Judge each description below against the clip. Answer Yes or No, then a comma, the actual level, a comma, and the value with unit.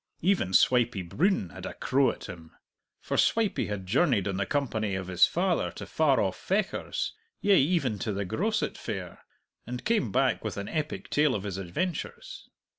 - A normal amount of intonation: No, wide, 8.9 semitones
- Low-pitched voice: Yes, low, 115 Hz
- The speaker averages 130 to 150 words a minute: No, average, 180 wpm